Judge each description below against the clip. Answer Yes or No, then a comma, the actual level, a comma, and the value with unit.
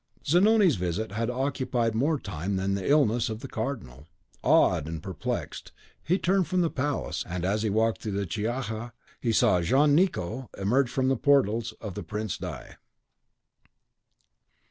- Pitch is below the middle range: Yes, low, 115 Hz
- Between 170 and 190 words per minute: No, average, 160 wpm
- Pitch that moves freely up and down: Yes, wide, 5.9 semitones